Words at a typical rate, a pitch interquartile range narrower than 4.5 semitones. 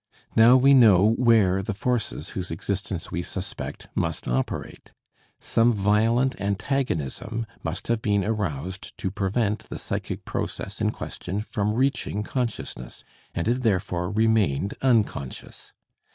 No: slow, 125 wpm; average, 3.8 semitones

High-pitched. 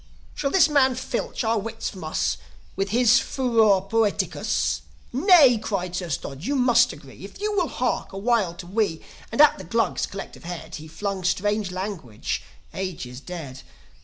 Yes: high, 200 Hz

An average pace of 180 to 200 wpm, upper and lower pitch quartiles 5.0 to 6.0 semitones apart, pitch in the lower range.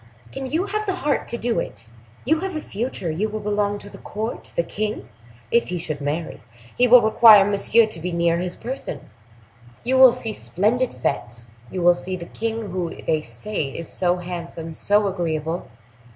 No: average, 185 wpm; wide, 5.6 semitones; high, 205 Hz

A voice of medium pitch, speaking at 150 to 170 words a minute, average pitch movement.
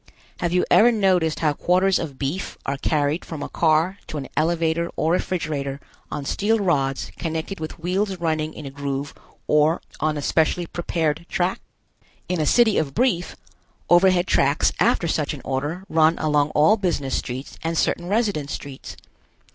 Yes: medium, 160 Hz; average, 165 wpm; average, 3.5 semitones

